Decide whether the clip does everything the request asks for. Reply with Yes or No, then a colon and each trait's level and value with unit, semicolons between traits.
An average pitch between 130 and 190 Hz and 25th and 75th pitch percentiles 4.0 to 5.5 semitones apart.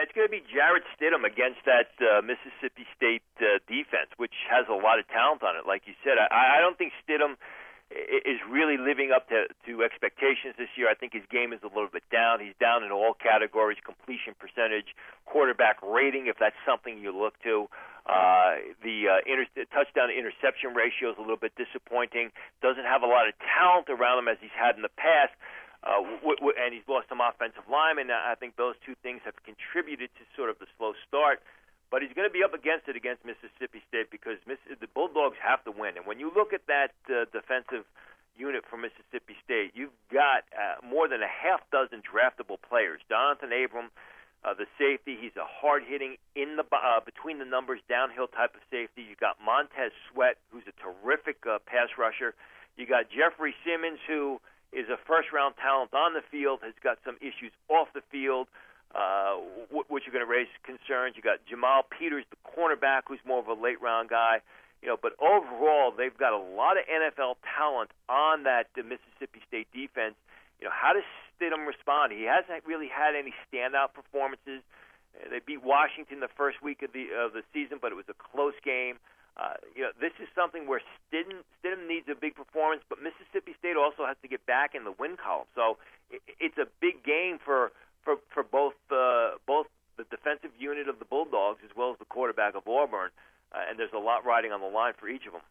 Yes: low, 135 Hz; average, 4.5 semitones